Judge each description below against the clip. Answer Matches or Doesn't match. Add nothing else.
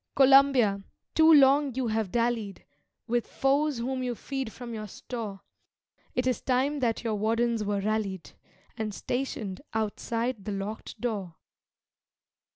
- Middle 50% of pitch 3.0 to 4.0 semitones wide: Matches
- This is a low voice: Doesn't match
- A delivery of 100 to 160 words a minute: Matches